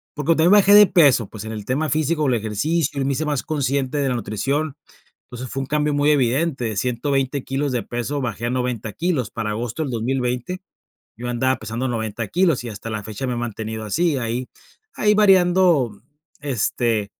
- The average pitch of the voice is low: Yes, low, 130 Hz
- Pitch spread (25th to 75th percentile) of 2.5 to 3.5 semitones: No, average, 4.5 semitones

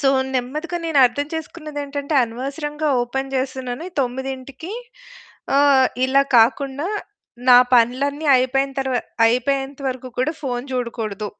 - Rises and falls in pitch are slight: Yes, narrow, 2.3 semitones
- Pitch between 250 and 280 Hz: Yes, very high, 270 Hz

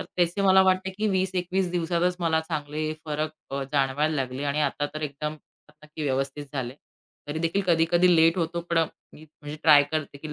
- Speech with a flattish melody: No, average, 3.1 semitones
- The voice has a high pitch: No, medium, 155 Hz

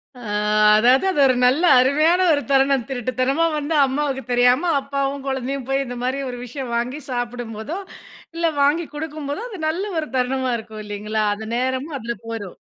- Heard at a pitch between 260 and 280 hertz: Yes, very high, 265 Hz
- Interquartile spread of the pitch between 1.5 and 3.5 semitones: Yes, average, 2.9 semitones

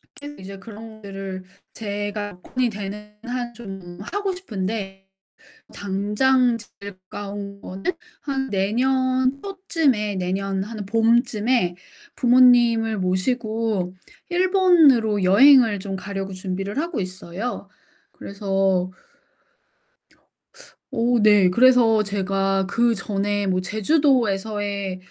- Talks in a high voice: Yes, high, 210 Hz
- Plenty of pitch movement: No, average, 4.0 semitones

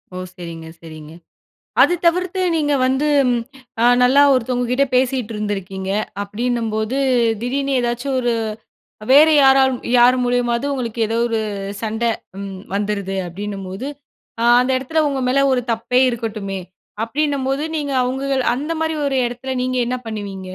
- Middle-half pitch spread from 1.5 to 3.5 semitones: No, average, 4.2 semitones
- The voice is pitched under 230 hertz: No, high, 245 Hz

